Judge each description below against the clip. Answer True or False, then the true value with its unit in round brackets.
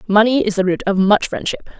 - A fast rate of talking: True (235 wpm)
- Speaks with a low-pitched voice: False (205 Hz)